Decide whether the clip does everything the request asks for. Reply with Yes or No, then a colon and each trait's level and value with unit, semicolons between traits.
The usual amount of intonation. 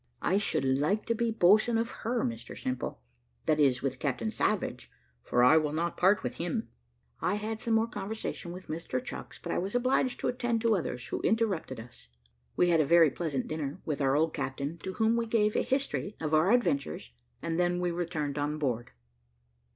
No: wide, 7.5 semitones